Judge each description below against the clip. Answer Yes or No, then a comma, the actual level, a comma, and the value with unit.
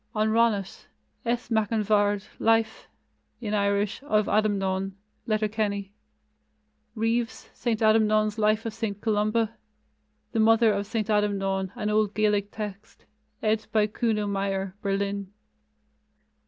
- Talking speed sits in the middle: No, slow, 120 wpm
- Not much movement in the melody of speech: Yes, narrow, 1.5 semitones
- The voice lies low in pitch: No, high, 215 Hz